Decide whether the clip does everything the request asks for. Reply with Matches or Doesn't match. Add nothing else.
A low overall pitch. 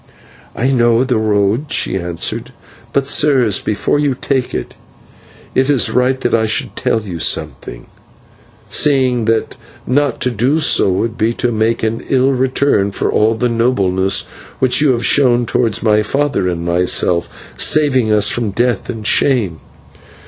Matches